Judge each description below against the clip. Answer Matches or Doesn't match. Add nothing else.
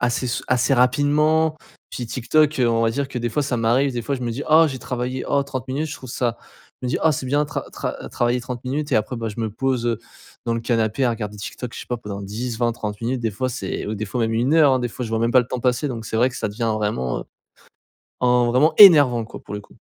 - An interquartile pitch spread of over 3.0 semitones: Doesn't match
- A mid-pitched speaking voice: Doesn't match